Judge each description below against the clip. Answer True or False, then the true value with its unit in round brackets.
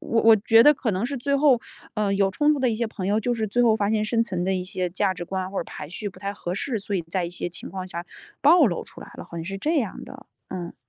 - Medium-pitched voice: False (205 Hz)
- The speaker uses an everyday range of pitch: True (4.1 semitones)